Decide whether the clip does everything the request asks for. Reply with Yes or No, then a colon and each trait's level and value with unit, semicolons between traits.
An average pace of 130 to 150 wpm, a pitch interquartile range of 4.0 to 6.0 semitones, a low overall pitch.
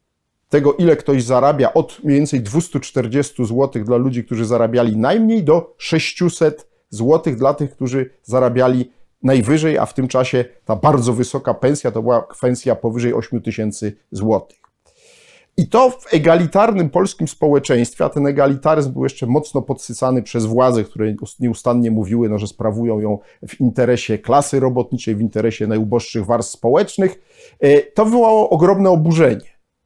Yes: average, 145 wpm; average, 4.9 semitones; low, 130 Hz